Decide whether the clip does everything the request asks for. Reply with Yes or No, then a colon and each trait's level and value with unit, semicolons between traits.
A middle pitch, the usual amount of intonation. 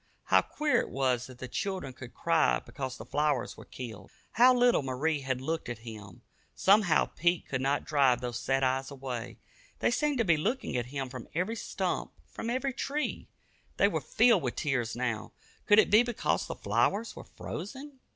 No: medium, 145 Hz; wide, 8.8 semitones